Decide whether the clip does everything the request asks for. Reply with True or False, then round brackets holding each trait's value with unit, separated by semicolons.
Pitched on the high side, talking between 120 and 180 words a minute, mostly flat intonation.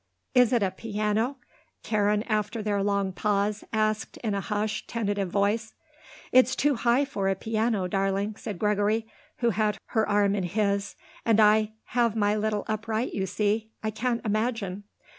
True (215 Hz; 160 wpm; 1.6 semitones)